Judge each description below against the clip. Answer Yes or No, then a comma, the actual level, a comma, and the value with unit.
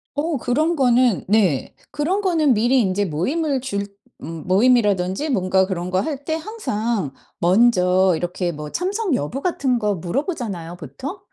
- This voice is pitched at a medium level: No, high, 220 Hz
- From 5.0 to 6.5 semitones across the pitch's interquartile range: No, wide, 7.7 semitones